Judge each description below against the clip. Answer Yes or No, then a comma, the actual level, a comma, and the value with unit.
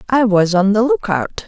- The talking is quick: Yes, fast, 245 wpm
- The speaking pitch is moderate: No, high, 225 Hz